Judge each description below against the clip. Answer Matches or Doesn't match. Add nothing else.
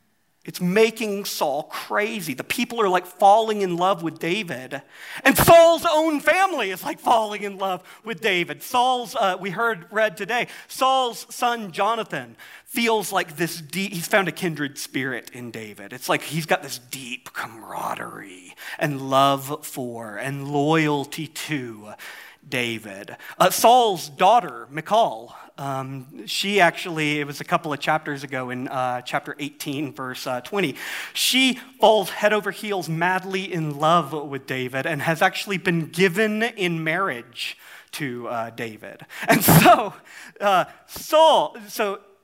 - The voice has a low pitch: Doesn't match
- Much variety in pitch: Matches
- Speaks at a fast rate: Doesn't match